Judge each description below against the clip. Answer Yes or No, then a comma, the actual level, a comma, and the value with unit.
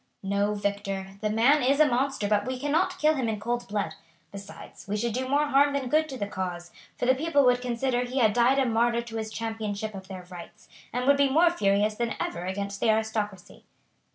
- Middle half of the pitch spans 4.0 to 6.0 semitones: Yes, average, 4.5 semitones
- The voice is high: Yes, high, 230 Hz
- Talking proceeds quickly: Yes, fast, 220 wpm